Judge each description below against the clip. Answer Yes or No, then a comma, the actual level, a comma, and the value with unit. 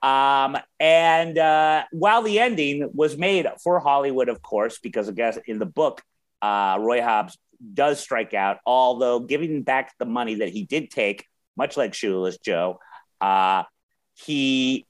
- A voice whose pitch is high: No, medium, 140 Hz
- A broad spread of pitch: No, average, 4.7 semitones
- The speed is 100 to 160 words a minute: Yes, average, 155 wpm